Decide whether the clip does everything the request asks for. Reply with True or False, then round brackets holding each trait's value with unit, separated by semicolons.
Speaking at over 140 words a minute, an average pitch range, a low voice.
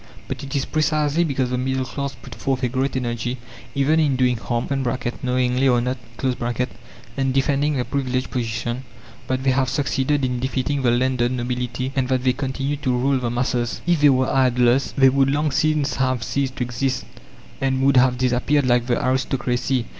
False (185 wpm; 1.6 semitones; 130 Hz)